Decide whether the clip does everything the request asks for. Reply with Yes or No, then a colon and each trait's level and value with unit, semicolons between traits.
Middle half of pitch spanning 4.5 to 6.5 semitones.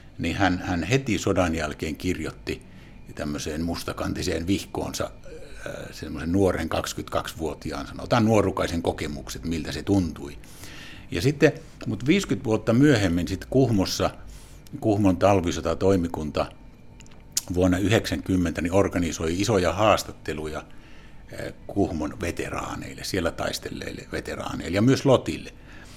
Yes: average, 5.0 semitones